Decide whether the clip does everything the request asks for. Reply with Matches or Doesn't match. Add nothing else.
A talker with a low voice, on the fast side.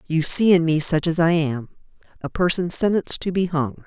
Doesn't match